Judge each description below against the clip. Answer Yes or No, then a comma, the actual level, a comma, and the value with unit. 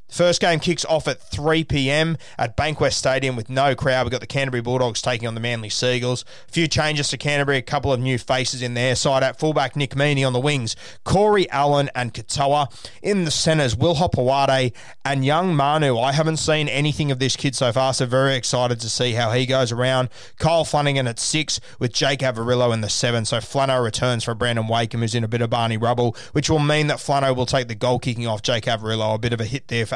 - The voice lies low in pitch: Yes, low, 130 Hz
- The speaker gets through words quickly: Yes, fast, 230 wpm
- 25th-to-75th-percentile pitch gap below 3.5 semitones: Yes, average, 3.0 semitones